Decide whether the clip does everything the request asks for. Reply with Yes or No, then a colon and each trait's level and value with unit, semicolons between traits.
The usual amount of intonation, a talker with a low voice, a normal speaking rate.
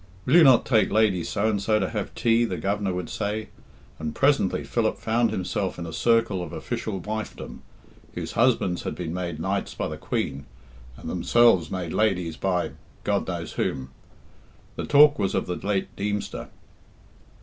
Yes: average, 4.0 semitones; low, 100 Hz; average, 170 wpm